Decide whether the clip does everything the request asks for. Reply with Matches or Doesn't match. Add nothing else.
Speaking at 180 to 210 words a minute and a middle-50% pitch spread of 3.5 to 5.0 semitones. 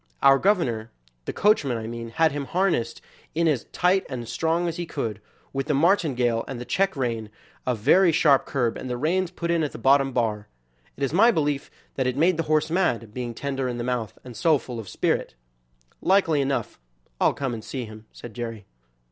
Doesn't match